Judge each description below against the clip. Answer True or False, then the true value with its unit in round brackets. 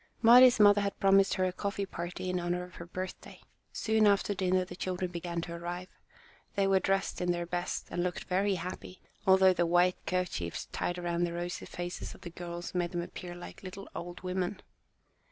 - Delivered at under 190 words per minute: False (195 wpm)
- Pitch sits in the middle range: True (180 Hz)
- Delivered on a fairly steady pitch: True (1.6 semitones)